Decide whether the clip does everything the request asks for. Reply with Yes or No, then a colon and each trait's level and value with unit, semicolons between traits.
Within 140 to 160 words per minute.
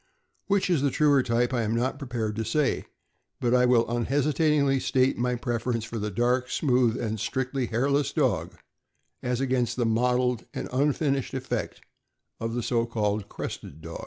No: average, 170 wpm